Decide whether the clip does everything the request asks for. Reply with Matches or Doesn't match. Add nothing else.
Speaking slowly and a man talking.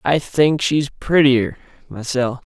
Matches